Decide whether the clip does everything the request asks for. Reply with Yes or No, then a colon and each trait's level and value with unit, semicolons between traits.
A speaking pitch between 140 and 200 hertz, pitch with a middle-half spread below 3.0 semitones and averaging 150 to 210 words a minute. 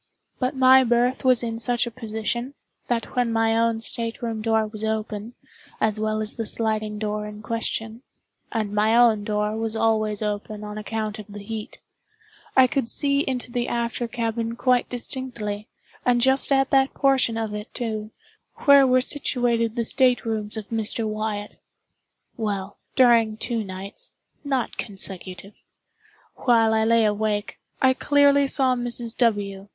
No: high, 225 Hz; narrow, 2.4 semitones; average, 155 wpm